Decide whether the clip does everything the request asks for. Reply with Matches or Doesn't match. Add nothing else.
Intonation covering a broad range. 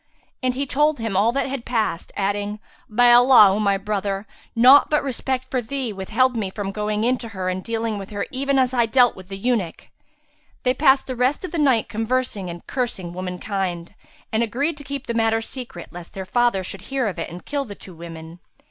Doesn't match